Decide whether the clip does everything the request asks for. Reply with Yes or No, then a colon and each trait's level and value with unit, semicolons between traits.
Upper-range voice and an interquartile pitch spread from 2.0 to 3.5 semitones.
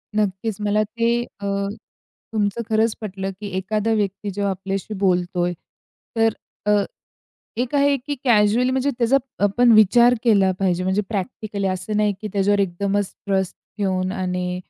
Yes: high, 205 Hz; narrow, 2.6 semitones